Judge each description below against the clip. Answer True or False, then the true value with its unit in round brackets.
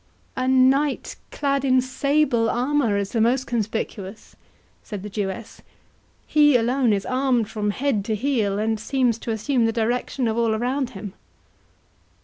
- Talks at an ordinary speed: True (150 wpm)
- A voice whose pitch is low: False (235 Hz)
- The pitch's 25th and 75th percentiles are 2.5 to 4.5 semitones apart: True (3.3 semitones)